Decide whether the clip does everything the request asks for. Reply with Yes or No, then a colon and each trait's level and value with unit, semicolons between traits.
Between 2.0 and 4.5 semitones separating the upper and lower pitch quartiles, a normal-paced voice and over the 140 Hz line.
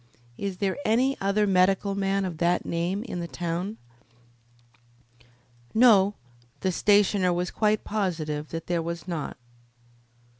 No: average, 3.0 semitones; slow, 125 wpm; high, 190 Hz